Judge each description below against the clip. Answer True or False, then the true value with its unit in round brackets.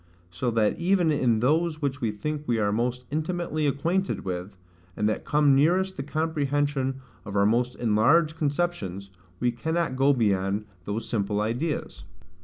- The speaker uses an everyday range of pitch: False (6.3 semitones)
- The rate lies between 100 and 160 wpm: True (155 wpm)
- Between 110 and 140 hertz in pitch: True (135 Hz)